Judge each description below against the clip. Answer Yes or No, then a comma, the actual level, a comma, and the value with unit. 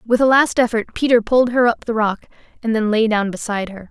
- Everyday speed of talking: No, fast, 245 wpm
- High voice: Yes, high, 225 Hz